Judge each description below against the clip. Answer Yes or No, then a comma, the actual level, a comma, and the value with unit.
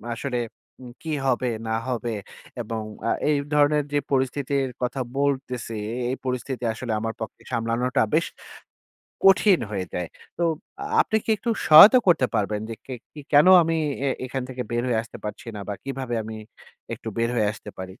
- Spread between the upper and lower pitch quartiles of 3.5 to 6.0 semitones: Yes, average, 4.0 semitones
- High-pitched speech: No, low, 125 Hz